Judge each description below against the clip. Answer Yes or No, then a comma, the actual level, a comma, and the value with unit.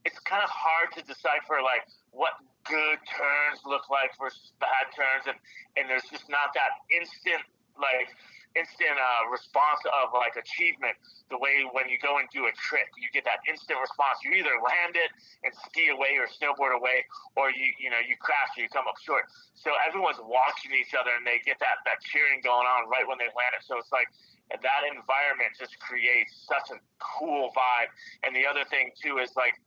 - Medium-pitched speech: Yes, medium, 145 Hz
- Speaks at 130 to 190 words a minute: No, average, 200 wpm